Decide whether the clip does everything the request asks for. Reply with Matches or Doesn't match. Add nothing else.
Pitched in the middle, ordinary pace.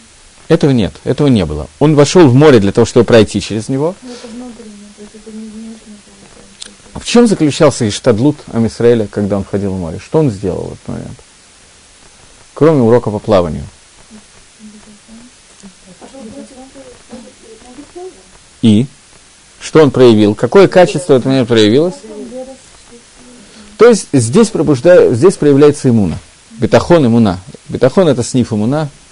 Matches